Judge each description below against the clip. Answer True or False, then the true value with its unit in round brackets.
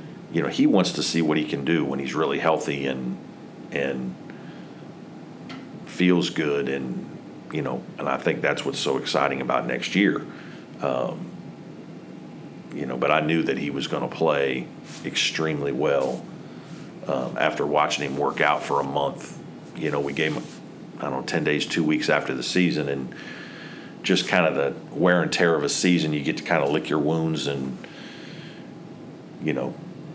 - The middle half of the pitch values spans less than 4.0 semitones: True (2.8 semitones)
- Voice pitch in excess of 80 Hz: False (70 Hz)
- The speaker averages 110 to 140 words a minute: False (180 wpm)